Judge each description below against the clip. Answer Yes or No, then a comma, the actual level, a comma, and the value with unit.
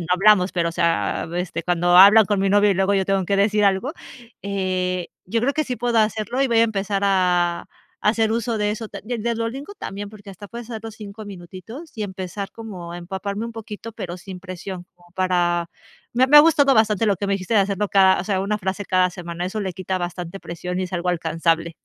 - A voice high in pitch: Yes, high, 195 Hz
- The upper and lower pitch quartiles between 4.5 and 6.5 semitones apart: No, average, 3.2 semitones